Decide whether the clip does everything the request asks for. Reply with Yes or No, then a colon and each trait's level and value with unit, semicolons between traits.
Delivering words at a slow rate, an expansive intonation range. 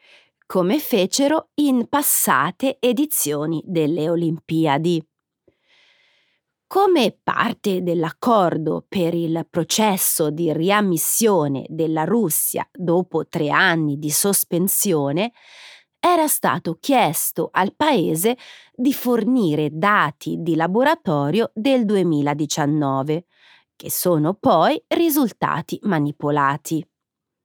Yes: slow, 85 wpm; wide, 7.1 semitones